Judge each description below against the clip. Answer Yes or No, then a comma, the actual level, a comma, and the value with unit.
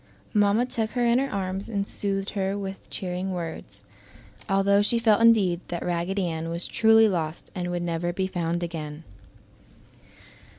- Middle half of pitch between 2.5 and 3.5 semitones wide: Yes, average, 3.0 semitones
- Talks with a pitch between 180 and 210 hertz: Yes, high, 190 Hz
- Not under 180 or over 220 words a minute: No, average, 160 wpm